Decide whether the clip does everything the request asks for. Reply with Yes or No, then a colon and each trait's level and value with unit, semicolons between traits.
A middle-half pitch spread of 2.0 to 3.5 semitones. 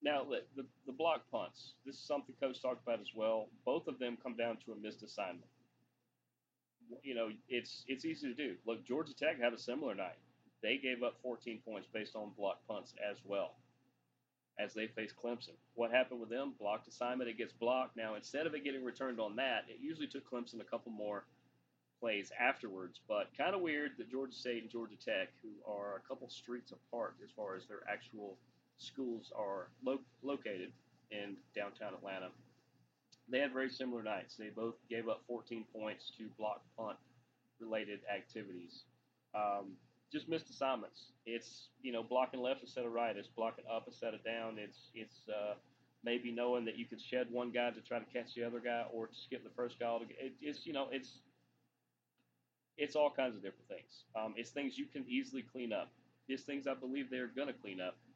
Yes: average, 2.8 semitones